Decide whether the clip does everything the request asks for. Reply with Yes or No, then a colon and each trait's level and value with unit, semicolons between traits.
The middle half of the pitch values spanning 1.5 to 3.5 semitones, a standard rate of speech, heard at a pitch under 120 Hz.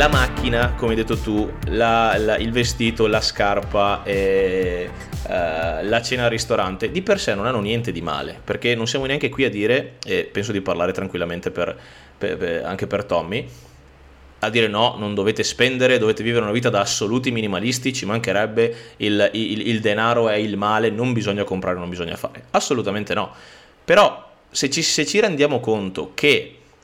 No: average, 2.8 semitones; fast, 185 wpm; low, 110 Hz